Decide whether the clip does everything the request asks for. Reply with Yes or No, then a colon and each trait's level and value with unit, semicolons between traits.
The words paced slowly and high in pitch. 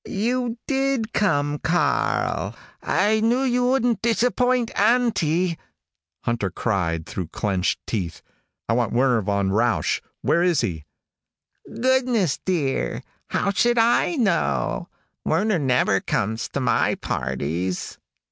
No: slow, 115 wpm; medium, 170 Hz